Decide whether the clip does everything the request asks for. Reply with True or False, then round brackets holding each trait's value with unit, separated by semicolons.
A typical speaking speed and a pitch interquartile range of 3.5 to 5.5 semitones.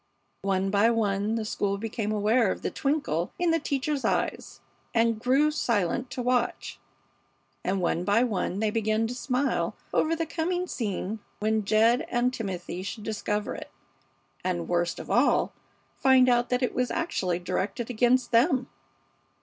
True (160 wpm; 4.0 semitones)